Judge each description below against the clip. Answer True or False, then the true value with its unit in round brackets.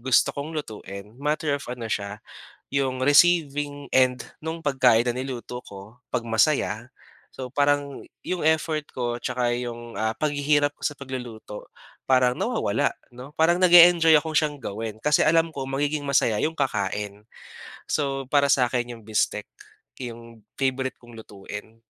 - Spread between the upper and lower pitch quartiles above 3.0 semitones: True (3.9 semitones)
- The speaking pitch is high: False (130 Hz)